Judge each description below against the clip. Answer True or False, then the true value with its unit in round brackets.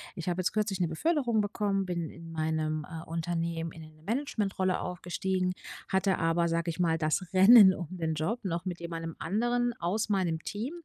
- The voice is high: False (180 Hz)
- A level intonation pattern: False (3.3 semitones)